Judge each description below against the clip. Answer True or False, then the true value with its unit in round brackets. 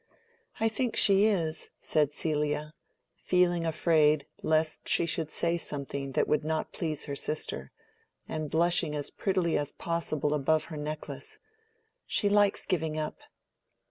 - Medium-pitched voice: True (155 Hz)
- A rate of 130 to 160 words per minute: True (140 wpm)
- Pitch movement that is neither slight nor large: False (2.3 semitones)